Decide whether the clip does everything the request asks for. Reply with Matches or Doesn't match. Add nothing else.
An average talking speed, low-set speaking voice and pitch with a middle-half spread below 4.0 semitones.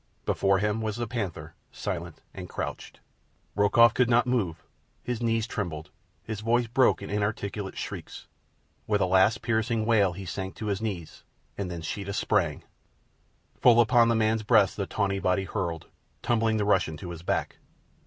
Matches